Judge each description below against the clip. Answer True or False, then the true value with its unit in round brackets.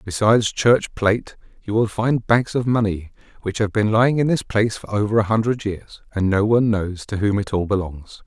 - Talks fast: True (220 wpm)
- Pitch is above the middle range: False (105 Hz)